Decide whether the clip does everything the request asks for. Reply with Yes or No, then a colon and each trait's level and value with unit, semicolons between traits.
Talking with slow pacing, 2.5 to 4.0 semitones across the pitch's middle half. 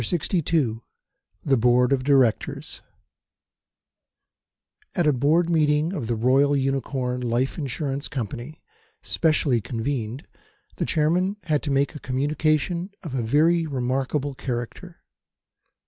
Yes: slow, 115 wpm; average, 3.7 semitones